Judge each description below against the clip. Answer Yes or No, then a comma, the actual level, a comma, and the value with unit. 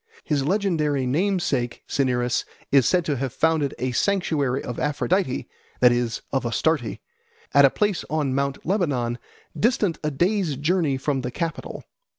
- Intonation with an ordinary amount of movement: Yes, average, 4.9 semitones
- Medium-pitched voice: Yes, medium, 145 Hz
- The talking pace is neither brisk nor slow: Yes, average, 150 wpm